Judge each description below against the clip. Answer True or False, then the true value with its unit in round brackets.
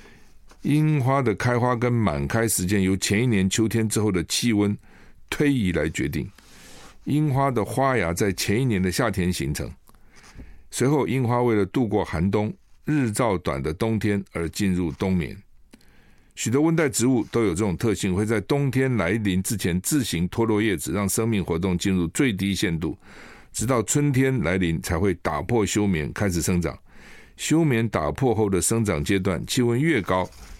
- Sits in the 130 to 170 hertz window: False (105 Hz)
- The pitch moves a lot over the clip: False (4.7 semitones)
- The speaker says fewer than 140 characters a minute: False (250 characters per minute)